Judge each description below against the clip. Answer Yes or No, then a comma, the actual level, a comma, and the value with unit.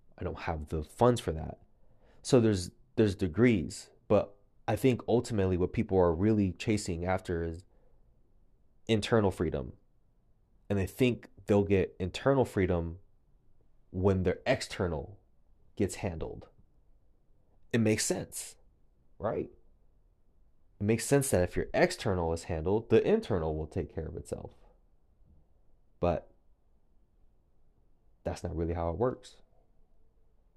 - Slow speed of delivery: Yes, slow, 125 wpm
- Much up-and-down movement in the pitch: No, average, 4.6 semitones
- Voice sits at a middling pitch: No, very low, 95 Hz